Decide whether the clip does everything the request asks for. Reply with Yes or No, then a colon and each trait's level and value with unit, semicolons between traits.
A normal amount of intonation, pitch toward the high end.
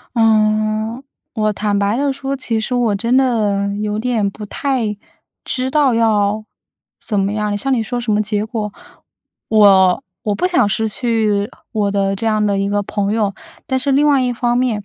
Yes: average, 3.0 semitones; high, 215 Hz